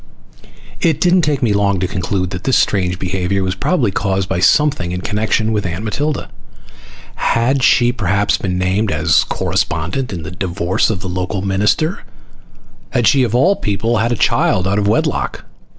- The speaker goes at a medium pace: Yes, average, 175 wpm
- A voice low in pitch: Yes, low, 100 Hz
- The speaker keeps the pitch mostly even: No, average, 4.5 semitones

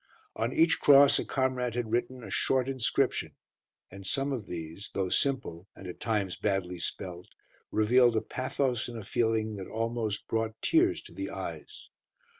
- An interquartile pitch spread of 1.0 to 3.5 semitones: No, average, 4.6 semitones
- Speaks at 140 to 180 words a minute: Yes, average, 165 wpm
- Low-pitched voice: Yes, low, 115 Hz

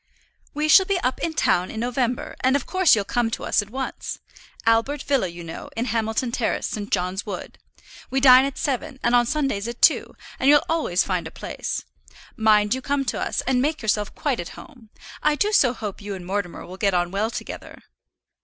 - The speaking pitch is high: Yes, high, 240 Hz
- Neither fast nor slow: No, fast, 210 wpm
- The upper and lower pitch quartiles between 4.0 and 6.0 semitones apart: Yes, average, 5.0 semitones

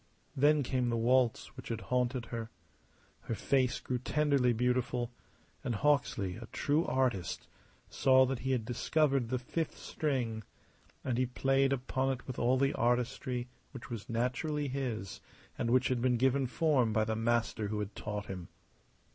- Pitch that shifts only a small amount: Yes, narrow, 2.3 semitones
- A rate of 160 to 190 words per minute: Yes, average, 165 wpm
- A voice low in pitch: Yes, low, 125 Hz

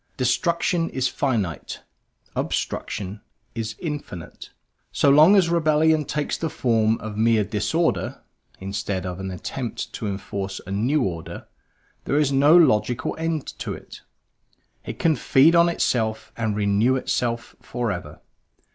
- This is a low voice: Yes, low, 120 Hz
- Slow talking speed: Yes, slow, 130 wpm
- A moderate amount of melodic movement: No, wide, 6.8 semitones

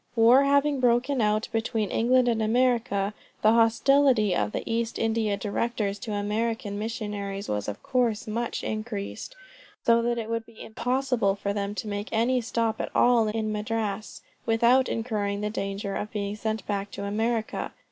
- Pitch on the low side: No, high, 225 Hz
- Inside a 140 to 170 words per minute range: Yes, average, 165 wpm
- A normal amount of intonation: No, narrow, 2.3 semitones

